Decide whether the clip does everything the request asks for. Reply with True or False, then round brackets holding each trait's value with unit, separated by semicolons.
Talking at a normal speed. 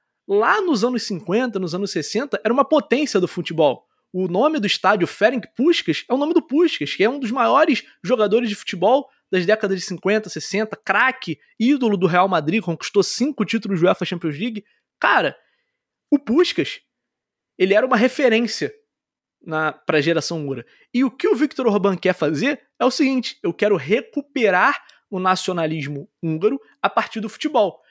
True (170 wpm)